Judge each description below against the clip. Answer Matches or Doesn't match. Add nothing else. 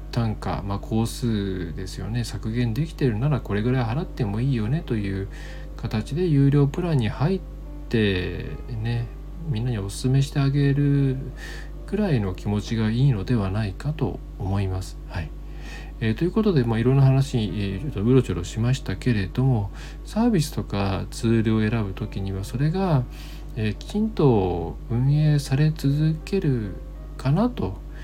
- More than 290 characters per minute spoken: Matches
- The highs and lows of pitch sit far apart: Matches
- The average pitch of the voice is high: Doesn't match